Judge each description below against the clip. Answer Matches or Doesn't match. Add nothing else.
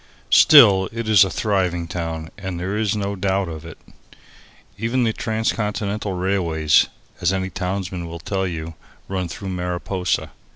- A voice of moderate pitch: Doesn't match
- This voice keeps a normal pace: Matches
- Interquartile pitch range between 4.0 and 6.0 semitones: Doesn't match